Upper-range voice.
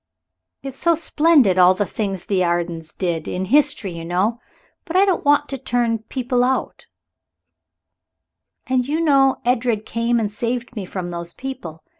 Yes: high, 230 Hz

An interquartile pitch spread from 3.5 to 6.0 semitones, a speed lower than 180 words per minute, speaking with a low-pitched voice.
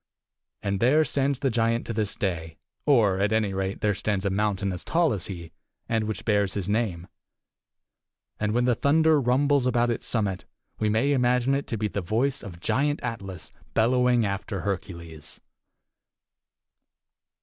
Yes: average, 4.3 semitones; average, 160 wpm; low, 110 Hz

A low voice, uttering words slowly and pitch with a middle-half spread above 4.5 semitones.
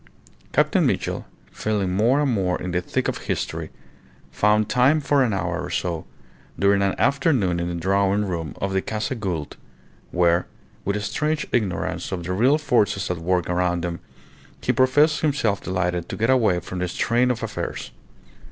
No: low, 100 Hz; average, 175 wpm; wide, 5.4 semitones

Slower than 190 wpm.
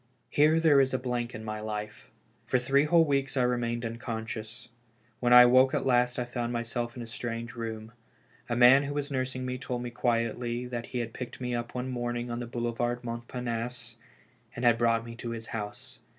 No: fast, 205 wpm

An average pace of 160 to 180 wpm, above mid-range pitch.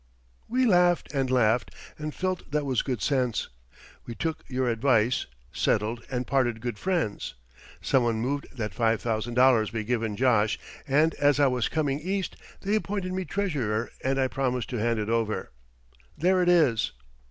No: average, 170 wpm; low, 130 Hz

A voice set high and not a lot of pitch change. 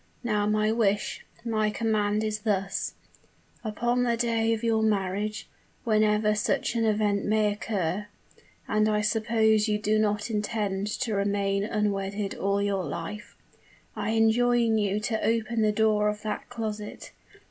Yes: high, 215 Hz; narrow, 1.3 semitones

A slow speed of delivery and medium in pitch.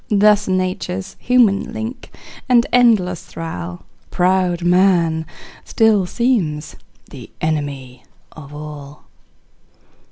Yes: slow, 90 wpm; medium, 180 Hz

